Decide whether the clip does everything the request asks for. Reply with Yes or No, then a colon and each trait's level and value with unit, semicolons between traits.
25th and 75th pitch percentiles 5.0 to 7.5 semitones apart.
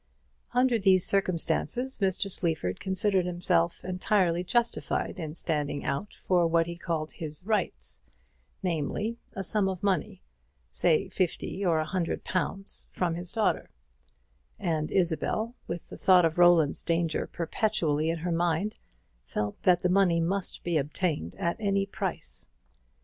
No: average, 3.2 semitones